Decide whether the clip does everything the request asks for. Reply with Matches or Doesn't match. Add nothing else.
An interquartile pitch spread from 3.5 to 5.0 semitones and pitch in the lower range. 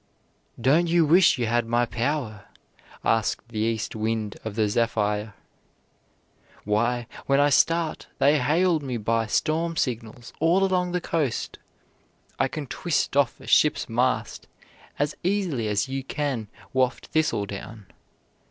Doesn't match